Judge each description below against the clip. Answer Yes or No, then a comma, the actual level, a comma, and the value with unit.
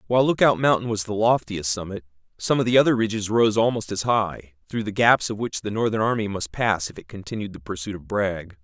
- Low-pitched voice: Yes, low, 105 Hz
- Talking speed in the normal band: No, fast, 230 wpm